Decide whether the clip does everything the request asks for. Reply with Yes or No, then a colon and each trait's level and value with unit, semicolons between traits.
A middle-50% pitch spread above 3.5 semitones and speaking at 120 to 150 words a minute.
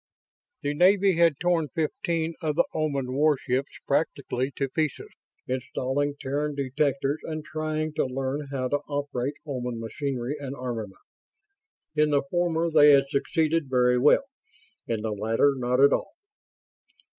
No: average, 3.2 semitones; average, 140 wpm